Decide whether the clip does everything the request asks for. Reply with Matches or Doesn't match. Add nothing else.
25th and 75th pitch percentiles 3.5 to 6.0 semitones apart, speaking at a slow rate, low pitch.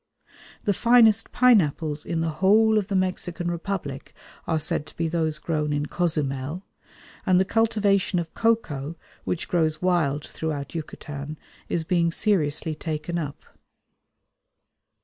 Doesn't match